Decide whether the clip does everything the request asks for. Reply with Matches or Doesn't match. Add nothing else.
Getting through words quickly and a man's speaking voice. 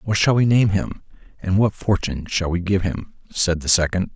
Matches